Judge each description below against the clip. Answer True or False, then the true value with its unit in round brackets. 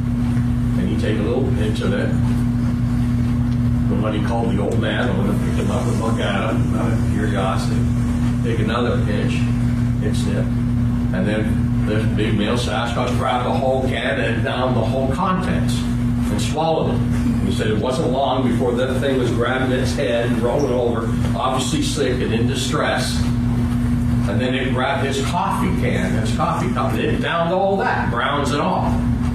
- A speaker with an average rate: True (175 wpm)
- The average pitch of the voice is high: False (120 Hz)